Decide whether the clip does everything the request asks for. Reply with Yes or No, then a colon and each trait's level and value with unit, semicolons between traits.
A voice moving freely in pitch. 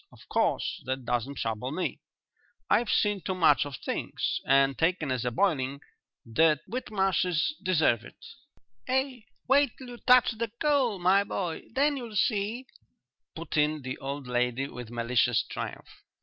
Yes: wide, 8.9 semitones